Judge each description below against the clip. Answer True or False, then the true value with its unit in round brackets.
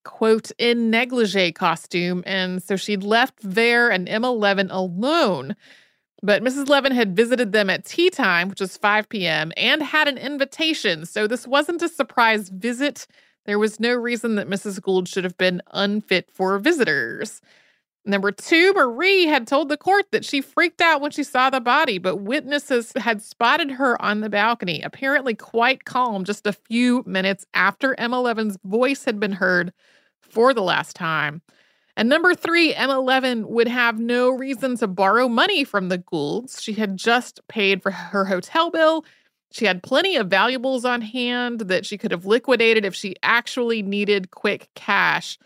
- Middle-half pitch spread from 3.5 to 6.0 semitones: True (5.0 semitones)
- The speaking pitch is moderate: False (230 Hz)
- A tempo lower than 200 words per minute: True (170 wpm)